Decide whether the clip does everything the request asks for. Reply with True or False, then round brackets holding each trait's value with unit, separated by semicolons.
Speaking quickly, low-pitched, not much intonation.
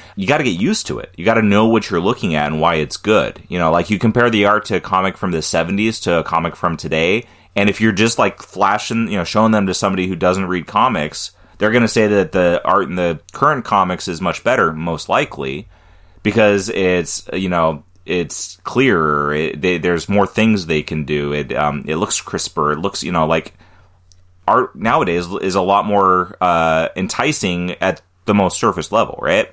False (215 wpm; 90 Hz; 3.5 semitones)